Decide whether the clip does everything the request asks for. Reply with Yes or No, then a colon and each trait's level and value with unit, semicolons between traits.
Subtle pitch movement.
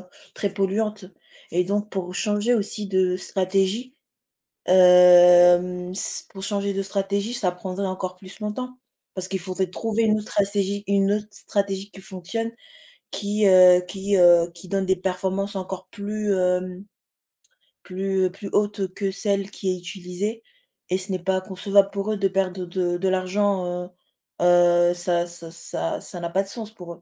Yes: narrow, 1.9 semitones